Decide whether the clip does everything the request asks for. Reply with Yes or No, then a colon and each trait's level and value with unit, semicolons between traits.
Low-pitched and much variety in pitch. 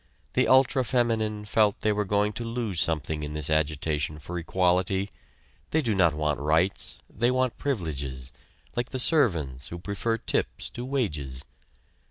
Yes: very low, 95 Hz; wide, 7.1 semitones